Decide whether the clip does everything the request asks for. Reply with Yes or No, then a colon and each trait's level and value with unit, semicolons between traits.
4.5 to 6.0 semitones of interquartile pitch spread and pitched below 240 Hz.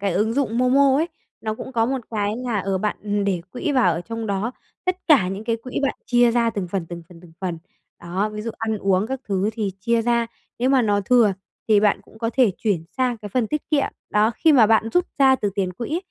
No: average, 3.9 semitones; high, 220 Hz